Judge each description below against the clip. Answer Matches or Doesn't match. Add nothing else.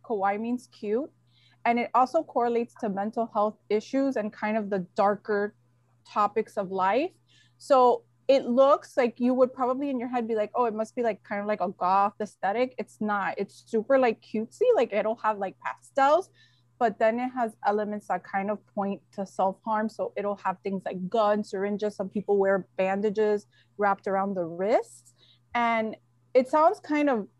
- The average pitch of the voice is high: Matches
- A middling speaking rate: Matches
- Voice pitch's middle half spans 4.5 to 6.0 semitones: Doesn't match